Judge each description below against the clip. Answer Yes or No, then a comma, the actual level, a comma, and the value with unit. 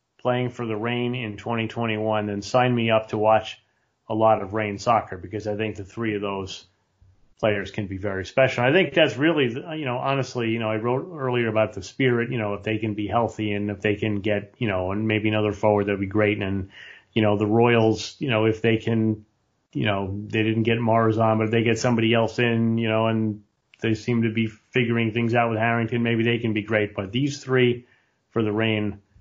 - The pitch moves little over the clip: Yes, narrow, 2.0 semitones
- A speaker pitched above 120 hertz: No, low, 110 Hz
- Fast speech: Yes, fast, 230 wpm